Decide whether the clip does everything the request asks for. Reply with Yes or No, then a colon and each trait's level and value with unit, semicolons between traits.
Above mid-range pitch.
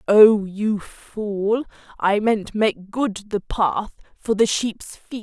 Yes: high, 210 Hz